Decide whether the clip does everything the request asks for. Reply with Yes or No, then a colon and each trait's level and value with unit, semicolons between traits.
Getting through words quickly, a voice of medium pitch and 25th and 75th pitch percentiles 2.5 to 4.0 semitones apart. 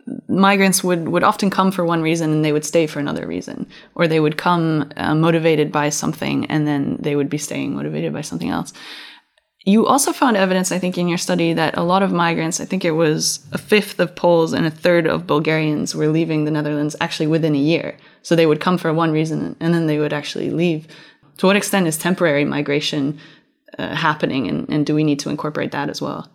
Yes: fast, 225 wpm; medium, 165 Hz; average, 2.8 semitones